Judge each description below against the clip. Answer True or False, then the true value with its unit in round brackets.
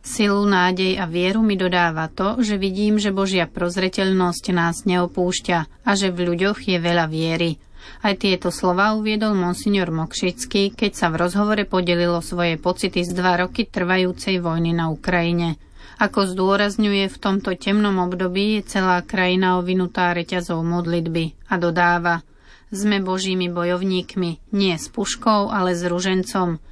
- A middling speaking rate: True (145 wpm)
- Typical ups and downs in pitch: False (2.3 semitones)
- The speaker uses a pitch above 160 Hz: True (185 Hz)